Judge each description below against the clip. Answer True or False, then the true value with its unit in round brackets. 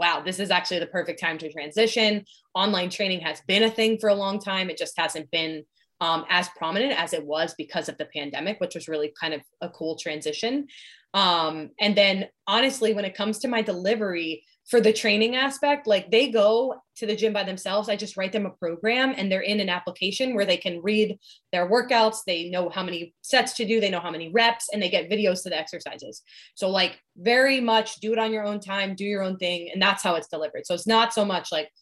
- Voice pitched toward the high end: True (195 Hz)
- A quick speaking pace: True (235 wpm)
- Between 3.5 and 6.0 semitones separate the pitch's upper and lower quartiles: True (4.2 semitones)